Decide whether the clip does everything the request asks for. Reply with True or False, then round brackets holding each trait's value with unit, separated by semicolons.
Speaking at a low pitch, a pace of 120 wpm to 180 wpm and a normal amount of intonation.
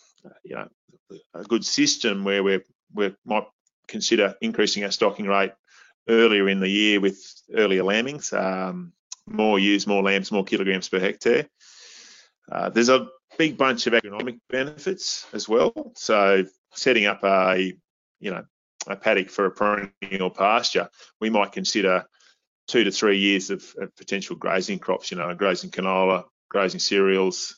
True (100 Hz; 155 wpm; 3.1 semitones)